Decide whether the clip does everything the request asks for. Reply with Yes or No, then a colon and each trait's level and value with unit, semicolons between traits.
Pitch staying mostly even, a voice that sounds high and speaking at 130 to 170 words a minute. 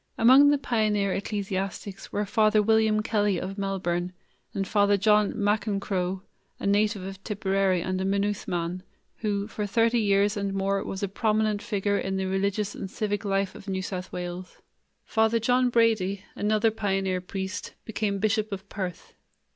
Yes: narrow, 1.9 semitones; high, 200 Hz; average, 160 wpm